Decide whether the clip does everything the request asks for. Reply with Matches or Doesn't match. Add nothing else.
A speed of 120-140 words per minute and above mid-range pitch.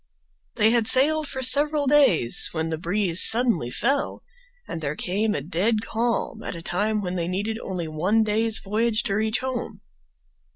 Doesn't match